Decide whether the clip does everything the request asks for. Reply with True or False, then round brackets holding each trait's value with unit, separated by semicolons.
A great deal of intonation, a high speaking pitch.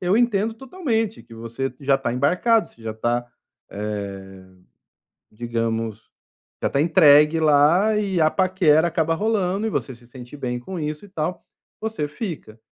False (8.2 semitones; 155 Hz)